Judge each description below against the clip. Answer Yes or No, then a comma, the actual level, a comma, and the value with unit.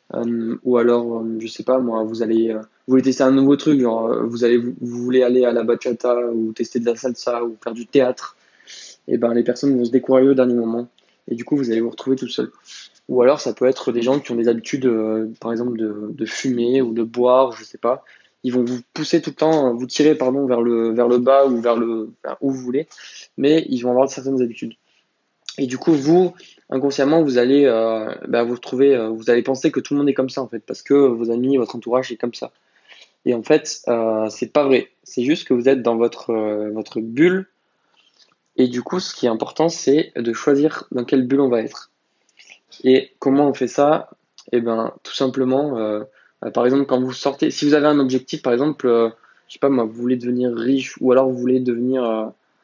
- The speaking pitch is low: Yes, low, 125 Hz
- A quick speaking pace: Yes, fast, 240 wpm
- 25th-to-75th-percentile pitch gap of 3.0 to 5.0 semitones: No, narrow, 2.5 semitones